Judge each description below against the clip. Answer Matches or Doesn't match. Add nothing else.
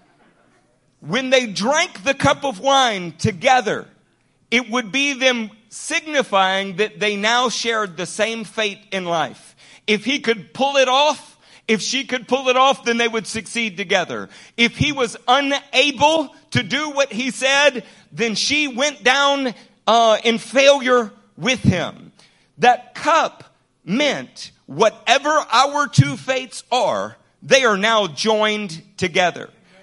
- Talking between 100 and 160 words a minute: Matches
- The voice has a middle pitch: Doesn't match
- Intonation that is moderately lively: Matches